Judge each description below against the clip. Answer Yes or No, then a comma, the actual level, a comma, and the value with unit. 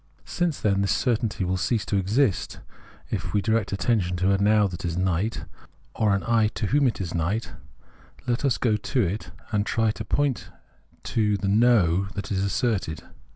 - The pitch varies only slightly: No, average, 3.0 semitones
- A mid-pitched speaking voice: No, low, 105 Hz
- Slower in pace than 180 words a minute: No, average, 190 wpm